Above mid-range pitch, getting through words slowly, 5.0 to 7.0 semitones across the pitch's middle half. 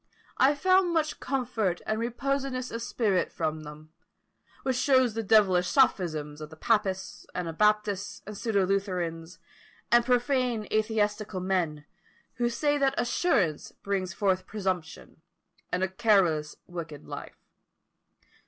Yes: high, 205 Hz; slow, 125 wpm; average, 5.3 semitones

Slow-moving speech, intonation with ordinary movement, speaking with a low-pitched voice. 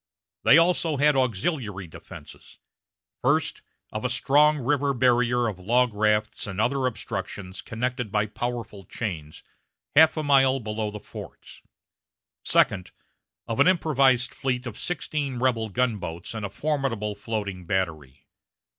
Yes: slow, 130 wpm; average, 4.7 semitones; low, 120 Hz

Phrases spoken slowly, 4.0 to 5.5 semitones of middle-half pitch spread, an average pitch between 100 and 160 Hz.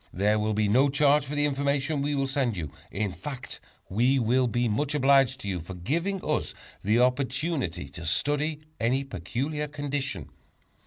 No: average, 170 wpm; average, 5.1 semitones; low, 135 Hz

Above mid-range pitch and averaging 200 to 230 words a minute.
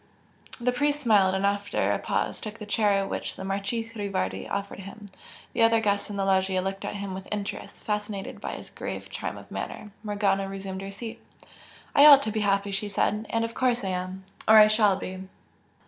Yes: high, 200 Hz; fast, 205 wpm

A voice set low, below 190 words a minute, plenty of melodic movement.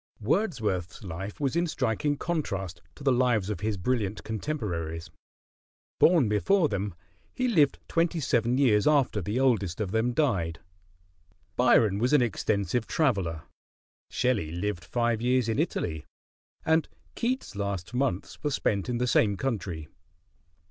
Yes: low, 115 Hz; average, 140 wpm; wide, 5.9 semitones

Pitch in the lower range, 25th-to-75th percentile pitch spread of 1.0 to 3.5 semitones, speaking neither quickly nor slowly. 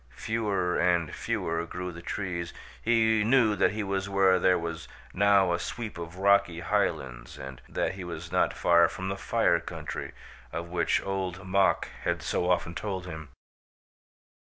Yes: very low, 90 Hz; narrow, 2.6 semitones; average, 160 wpm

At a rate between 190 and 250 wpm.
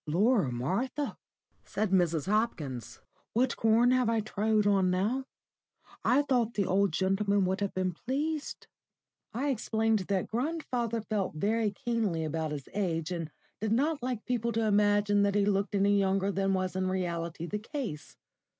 No: average, 160 wpm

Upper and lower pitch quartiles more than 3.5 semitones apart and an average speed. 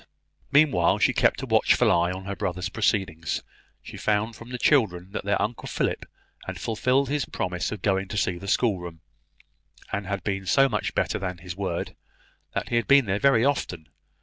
Yes: average, 4.4 semitones; average, 190 wpm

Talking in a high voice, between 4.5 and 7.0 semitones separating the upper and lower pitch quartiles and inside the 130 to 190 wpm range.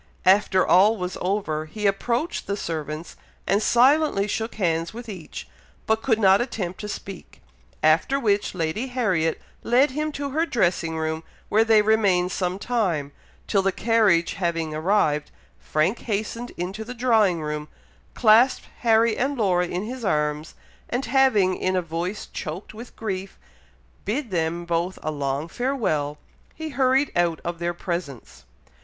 Yes: high, 195 Hz; wide, 5.5 semitones; average, 150 wpm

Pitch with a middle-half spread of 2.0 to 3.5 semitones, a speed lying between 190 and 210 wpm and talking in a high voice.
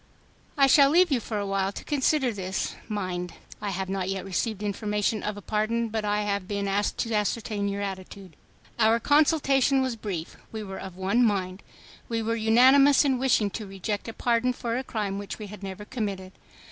Yes: average, 3.2 semitones; average, 195 wpm; high, 210 Hz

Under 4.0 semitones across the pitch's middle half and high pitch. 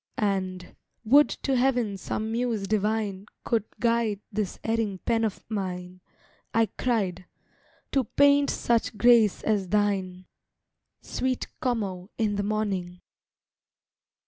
Yes: average, 3.3 semitones; high, 215 Hz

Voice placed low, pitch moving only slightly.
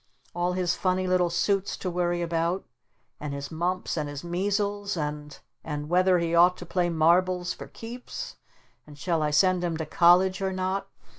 No: medium, 175 Hz; narrow, 2.2 semitones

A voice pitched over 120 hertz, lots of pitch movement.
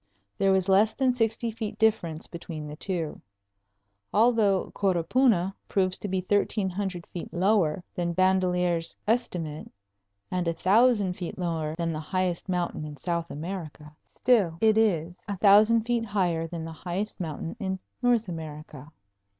No: medium, 185 Hz; average, 3.9 semitones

